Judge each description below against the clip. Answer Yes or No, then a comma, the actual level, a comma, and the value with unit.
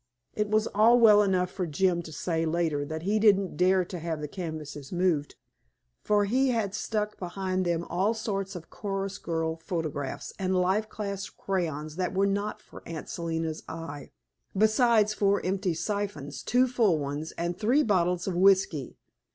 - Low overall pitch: No, medium, 185 Hz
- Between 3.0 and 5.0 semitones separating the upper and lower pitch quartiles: Yes, average, 4.0 semitones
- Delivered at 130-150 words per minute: No, average, 170 wpm